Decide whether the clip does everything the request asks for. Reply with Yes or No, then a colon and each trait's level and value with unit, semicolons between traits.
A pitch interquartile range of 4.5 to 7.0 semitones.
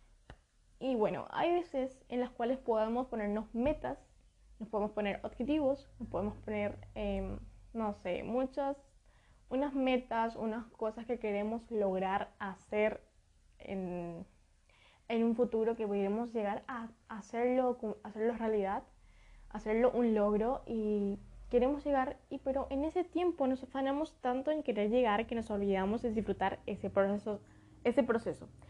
No: average, 4.1 semitones